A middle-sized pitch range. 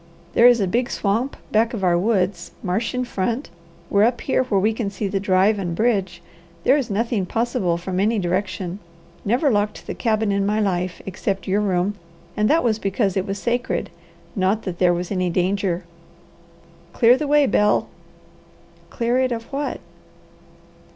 Yes: average, 3.8 semitones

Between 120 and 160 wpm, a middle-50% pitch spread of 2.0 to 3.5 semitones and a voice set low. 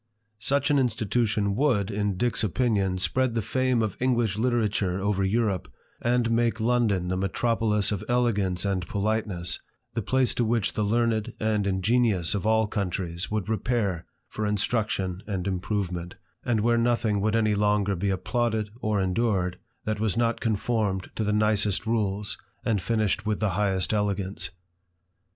Yes: average, 155 wpm; average, 2.9 semitones; low, 105 Hz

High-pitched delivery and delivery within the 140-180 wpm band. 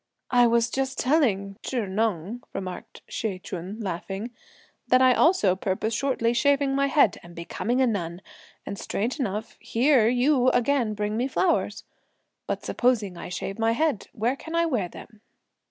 Yes: high, 230 Hz; average, 160 wpm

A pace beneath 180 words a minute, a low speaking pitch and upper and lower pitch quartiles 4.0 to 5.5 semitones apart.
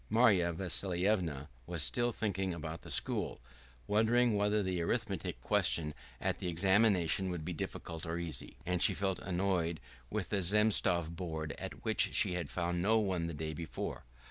No: average, 165 wpm; very low, 90 Hz; average, 3.3 semitones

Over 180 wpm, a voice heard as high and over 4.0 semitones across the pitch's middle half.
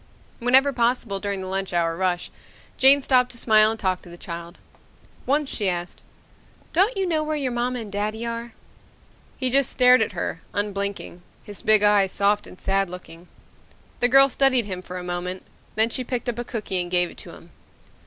Yes: average, 195 wpm; high, 215 Hz; average, 5.1 semitones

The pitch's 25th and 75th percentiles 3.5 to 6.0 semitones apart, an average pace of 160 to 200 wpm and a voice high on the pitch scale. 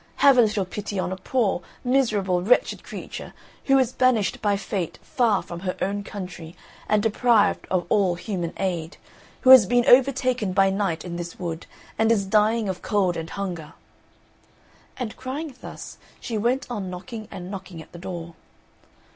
Yes: average, 4.5 semitones; average, 170 wpm; high, 200 Hz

